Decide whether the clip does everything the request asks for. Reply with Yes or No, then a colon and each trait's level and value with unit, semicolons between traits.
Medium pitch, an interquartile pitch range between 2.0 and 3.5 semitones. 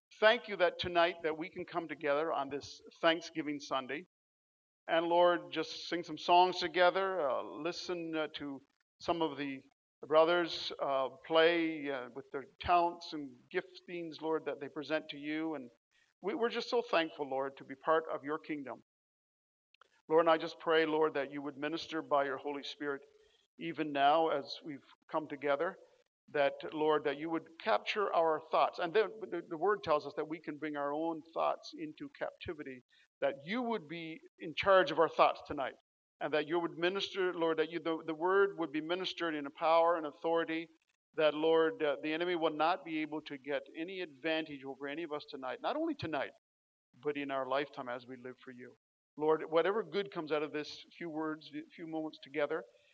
Yes: medium, 160 Hz; average, 2.7 semitones